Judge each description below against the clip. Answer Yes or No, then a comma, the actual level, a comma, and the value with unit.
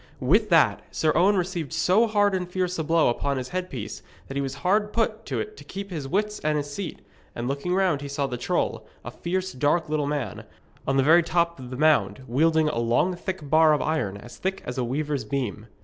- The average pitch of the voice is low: No, medium, 155 Hz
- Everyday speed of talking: No, fast, 225 wpm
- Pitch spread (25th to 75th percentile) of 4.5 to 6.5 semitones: Yes, average, 5.1 semitones